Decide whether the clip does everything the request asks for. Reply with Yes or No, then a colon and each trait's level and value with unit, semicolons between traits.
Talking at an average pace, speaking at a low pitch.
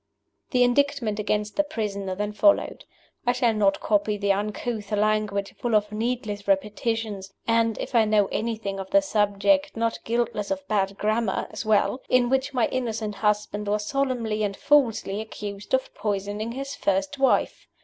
No: average, 160 wpm; high, 215 Hz